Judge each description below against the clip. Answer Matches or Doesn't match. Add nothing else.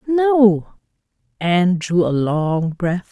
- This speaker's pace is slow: Matches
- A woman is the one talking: Matches